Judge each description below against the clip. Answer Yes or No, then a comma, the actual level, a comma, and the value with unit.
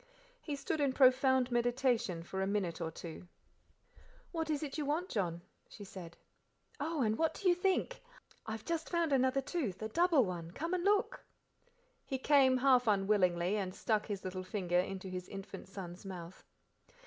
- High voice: Yes, high, 225 Hz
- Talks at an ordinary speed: Yes, average, 175 wpm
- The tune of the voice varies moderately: No, wide, 7.7 semitones